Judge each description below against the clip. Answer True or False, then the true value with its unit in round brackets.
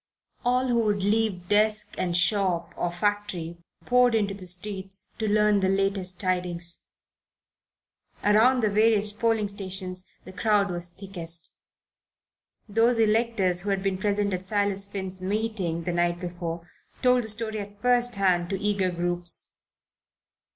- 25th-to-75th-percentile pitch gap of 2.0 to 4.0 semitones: True (2.9 semitones)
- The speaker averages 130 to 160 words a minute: True (145 wpm)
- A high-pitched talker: True (200 Hz)